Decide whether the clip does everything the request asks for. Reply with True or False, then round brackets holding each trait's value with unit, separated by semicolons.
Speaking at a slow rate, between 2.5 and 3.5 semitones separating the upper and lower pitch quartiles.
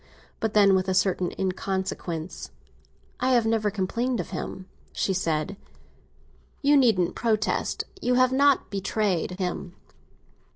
False (115 wpm; 4.2 semitones)